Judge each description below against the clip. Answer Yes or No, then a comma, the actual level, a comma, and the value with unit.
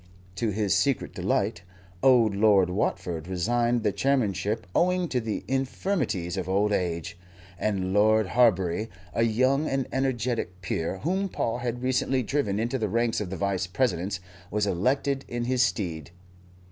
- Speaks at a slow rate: No, average, 150 wpm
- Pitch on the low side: Yes, low, 110 Hz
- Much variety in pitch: No, average, 5.0 semitones